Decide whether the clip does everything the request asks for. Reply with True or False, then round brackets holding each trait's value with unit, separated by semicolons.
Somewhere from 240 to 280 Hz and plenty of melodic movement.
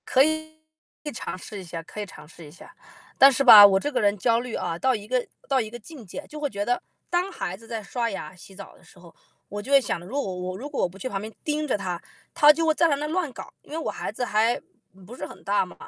False (230 Hz; 6.5 semitones)